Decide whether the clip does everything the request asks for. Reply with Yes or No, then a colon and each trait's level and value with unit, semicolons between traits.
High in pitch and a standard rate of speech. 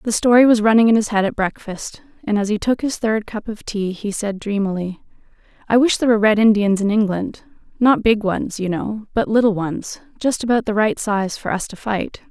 No: high, 215 Hz; fast, 225 wpm